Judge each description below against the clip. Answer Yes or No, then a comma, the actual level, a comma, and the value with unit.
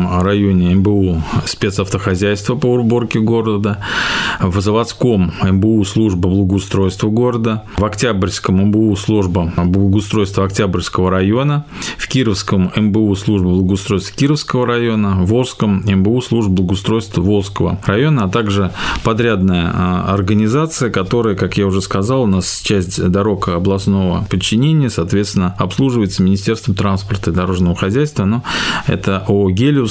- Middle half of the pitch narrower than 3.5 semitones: Yes, average, 3.1 semitones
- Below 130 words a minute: Yes, average, 120 wpm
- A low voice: Yes, low, 100 Hz